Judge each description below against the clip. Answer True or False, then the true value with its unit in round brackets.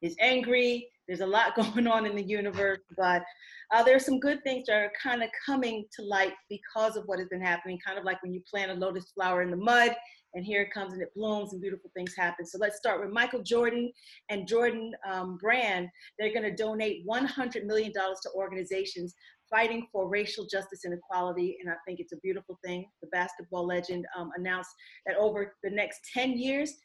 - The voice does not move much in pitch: False (3.9 semitones)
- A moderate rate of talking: False (210 wpm)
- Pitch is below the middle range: False (200 Hz)